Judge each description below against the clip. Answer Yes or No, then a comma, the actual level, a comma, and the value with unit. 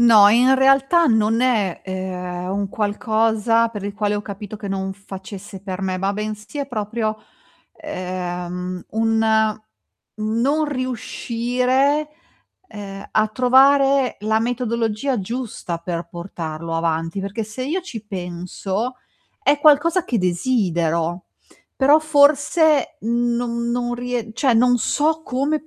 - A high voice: Yes, high, 220 Hz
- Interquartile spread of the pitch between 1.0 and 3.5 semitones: No, average, 4.9 semitones